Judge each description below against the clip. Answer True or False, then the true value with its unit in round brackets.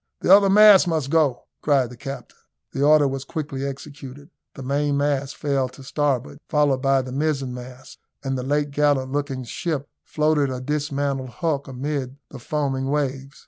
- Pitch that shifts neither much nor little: False (1.9 semitones)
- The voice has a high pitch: False (140 Hz)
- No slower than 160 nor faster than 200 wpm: True (165 wpm)